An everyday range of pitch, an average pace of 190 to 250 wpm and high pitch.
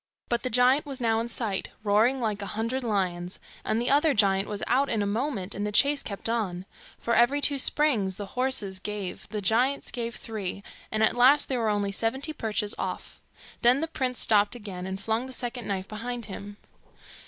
Yes: average, 3.7 semitones; average, 200 wpm; high, 225 Hz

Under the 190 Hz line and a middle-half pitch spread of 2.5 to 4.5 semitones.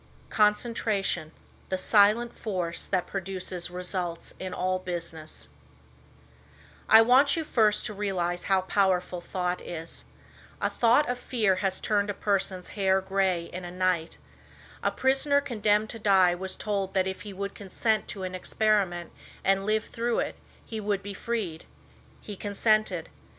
No: high, 195 Hz; average, 2.8 semitones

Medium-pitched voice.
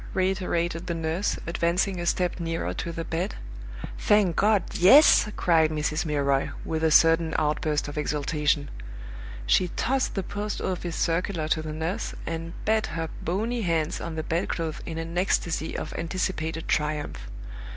Yes: medium, 165 Hz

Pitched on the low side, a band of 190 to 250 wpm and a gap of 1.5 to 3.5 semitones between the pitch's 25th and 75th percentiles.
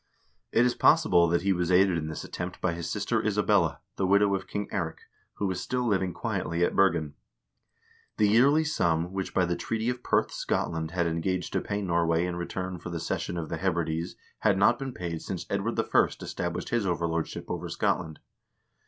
Yes: very low, 90 Hz; average, 195 wpm; average, 3.1 semitones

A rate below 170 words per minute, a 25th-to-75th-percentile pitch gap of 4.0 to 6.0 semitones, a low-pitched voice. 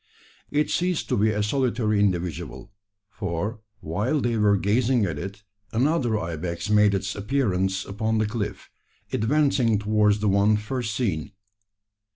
No: average, 140 wpm; average, 3.0 semitones; low, 105 Hz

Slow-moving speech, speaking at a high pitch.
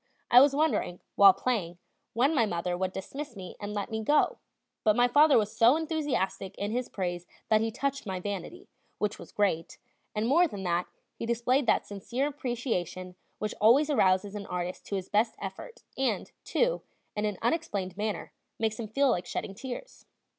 No: average, 180 wpm; high, 215 Hz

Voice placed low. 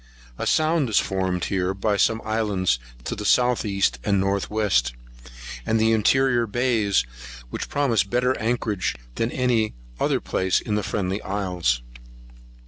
Yes: low, 105 Hz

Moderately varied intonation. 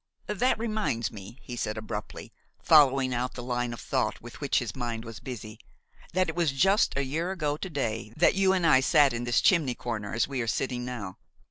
No: wide, 5.7 semitones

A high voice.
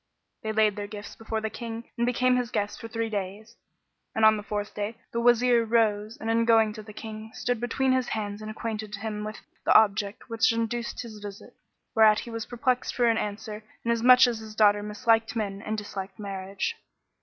Yes: high, 220 Hz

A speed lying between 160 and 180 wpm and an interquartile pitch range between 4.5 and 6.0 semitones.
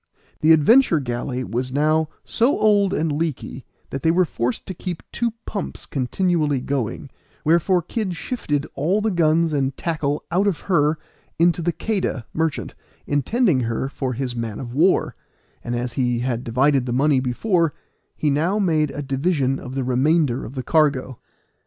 Yes: average, 165 wpm; average, 4.9 semitones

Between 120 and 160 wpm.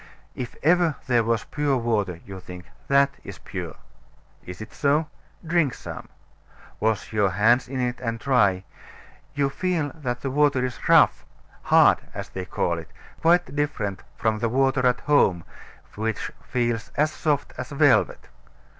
Yes: average, 155 wpm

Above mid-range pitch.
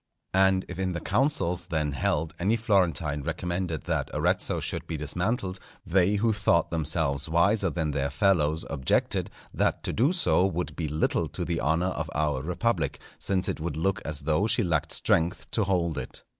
No: very low, 85 Hz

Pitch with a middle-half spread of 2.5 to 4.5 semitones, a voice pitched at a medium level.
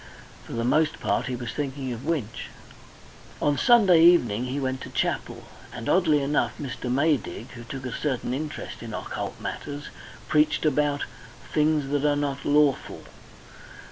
Yes: average, 2.9 semitones; medium, 145 Hz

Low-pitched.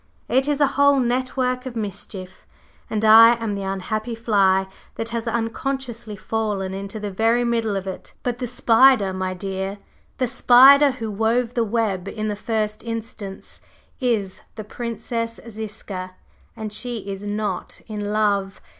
No: high, 220 Hz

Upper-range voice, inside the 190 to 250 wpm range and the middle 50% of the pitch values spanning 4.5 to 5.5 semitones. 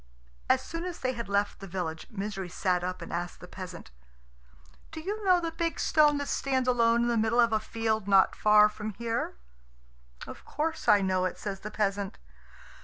Yes: high, 215 Hz; average, 195 wpm; average, 5.0 semitones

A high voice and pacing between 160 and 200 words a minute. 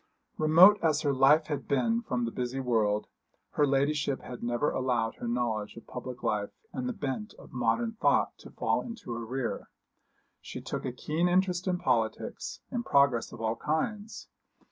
No: low, 135 Hz; average, 170 wpm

